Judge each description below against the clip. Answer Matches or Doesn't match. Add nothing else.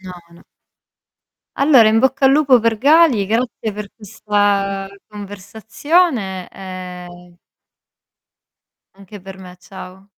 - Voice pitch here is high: Matches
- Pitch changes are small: Doesn't match